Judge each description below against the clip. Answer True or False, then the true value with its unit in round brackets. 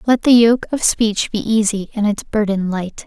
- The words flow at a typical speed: False (215 wpm)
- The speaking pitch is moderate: False (215 Hz)